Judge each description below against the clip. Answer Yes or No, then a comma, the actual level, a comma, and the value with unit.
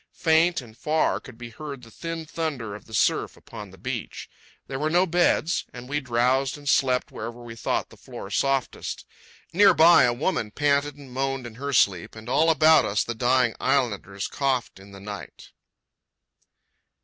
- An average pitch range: Yes, average, 4.6 semitones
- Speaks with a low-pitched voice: Yes, low, 130 Hz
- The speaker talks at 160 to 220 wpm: Yes, average, 180 wpm